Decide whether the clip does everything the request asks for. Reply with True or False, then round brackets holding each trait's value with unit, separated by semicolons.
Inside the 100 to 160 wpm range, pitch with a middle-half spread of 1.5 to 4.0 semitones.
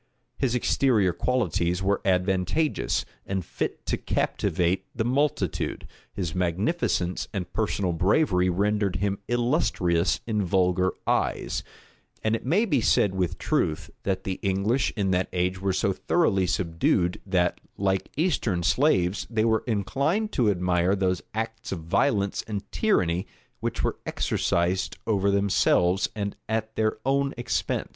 True (140 wpm; 3.7 semitones)